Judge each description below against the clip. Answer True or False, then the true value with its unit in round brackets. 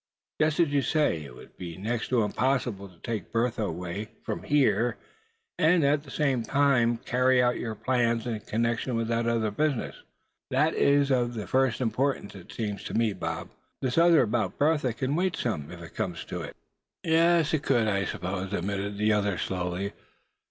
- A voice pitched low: True (115 Hz)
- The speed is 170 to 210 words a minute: True (185 wpm)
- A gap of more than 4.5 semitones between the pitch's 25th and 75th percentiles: True (5.1 semitones)